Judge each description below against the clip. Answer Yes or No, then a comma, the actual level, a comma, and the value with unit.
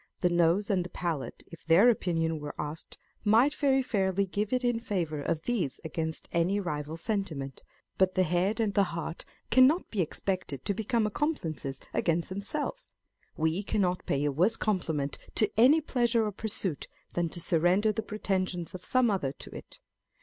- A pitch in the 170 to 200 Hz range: Yes, medium, 185 Hz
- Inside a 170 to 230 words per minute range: Yes, average, 175 wpm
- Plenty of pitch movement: No, average, 5.0 semitones